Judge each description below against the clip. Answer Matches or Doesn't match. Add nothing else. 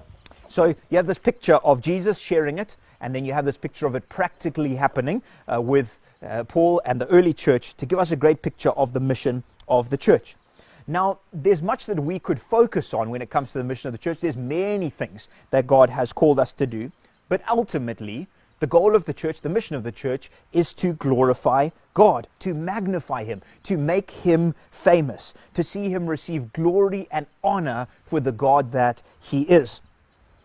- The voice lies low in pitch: Doesn't match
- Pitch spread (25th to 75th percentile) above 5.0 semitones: Matches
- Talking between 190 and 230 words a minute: Matches